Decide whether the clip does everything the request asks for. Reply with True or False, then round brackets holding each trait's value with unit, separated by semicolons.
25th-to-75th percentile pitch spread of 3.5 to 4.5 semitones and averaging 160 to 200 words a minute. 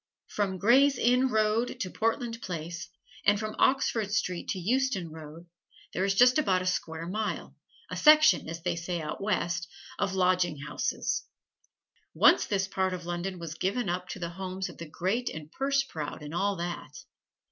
True (4.2 semitones; 175 wpm)